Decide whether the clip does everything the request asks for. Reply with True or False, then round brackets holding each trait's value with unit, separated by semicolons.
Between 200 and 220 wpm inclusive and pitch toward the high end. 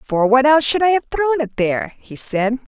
False (240 wpm; 270 Hz)